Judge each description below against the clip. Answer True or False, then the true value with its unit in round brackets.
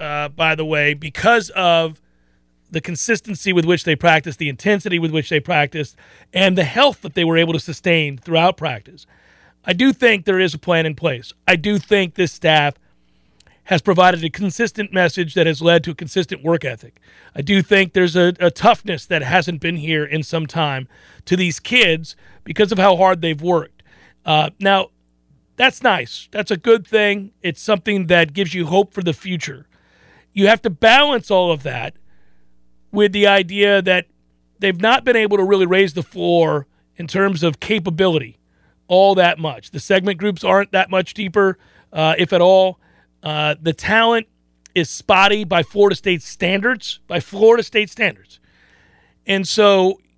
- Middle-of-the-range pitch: True (180 Hz)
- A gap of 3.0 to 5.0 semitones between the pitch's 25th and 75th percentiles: True (3.9 semitones)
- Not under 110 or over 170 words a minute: False (180 wpm)